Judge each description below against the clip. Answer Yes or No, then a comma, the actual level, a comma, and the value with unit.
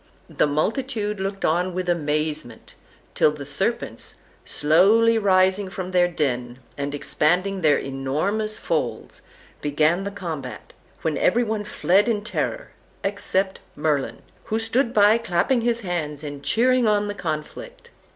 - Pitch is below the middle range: No, medium, 185 Hz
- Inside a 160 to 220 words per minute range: No, slow, 135 wpm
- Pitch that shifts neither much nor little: No, wide, 5.9 semitones